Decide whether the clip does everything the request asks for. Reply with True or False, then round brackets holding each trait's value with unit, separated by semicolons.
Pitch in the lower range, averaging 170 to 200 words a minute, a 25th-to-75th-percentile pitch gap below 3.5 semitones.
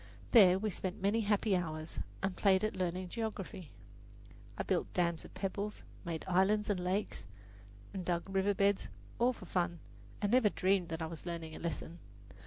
False (190 Hz; 175 wpm; 2.8 semitones)